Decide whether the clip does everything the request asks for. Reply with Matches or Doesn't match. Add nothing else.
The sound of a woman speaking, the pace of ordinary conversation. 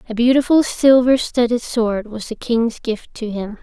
Matches